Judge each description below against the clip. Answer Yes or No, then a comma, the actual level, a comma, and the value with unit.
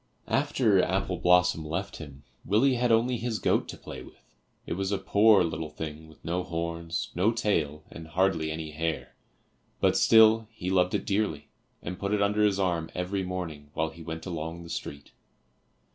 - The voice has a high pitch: No, very low, 90 Hz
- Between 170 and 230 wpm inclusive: Yes, average, 180 wpm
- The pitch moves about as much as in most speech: Yes, average, 4.0 semitones